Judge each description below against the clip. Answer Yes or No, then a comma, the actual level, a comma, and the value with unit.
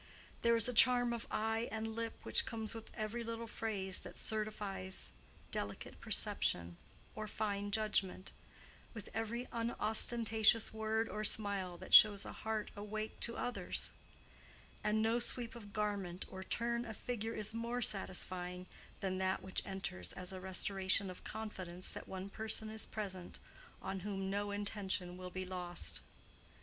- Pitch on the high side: Yes, high, 210 Hz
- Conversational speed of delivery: Yes, average, 150 wpm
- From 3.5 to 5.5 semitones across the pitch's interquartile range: No, average, 2.8 semitones